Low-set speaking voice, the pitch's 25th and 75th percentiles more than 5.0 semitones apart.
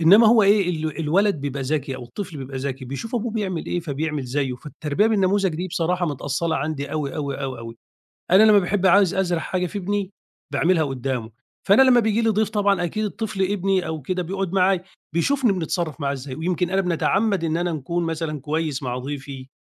No: medium, 170 Hz; wide, 5.4 semitones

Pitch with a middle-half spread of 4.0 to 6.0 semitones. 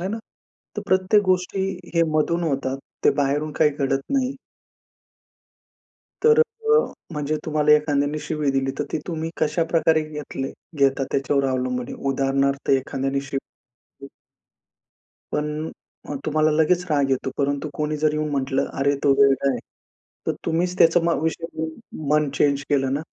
No: average, 2.8 semitones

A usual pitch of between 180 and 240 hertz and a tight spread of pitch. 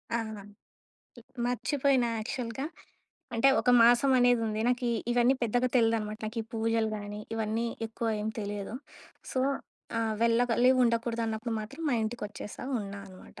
Yes: high, 230 Hz; narrow, 2.1 semitones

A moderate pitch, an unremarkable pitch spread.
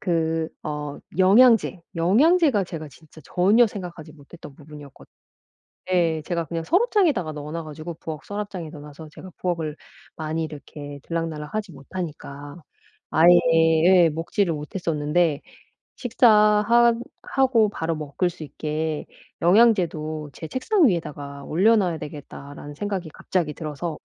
Yes: medium, 165 Hz; average, 4.4 semitones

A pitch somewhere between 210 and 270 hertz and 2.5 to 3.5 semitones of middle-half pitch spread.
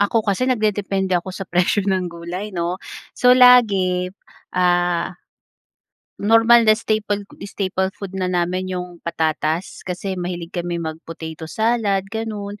No: medium, 185 Hz; average, 3.0 semitones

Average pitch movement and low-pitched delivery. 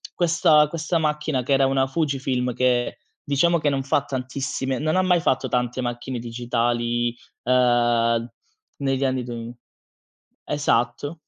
Yes: average, 3.3 semitones; low, 130 Hz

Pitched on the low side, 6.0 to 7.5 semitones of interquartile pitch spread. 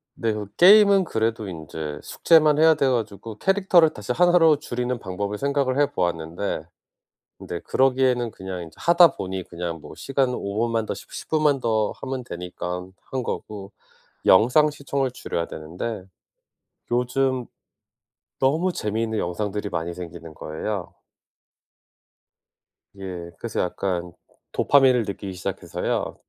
Yes: low, 110 Hz; wide, 6.7 semitones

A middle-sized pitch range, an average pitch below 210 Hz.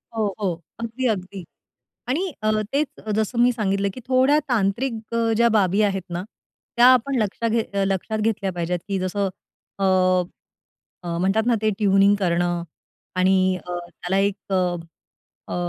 Yes: average, 3.5 semitones; high, 200 Hz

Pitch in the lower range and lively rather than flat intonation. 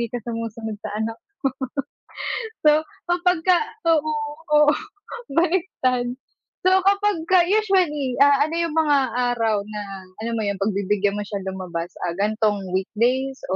No: high, 235 Hz; wide, 7.1 semitones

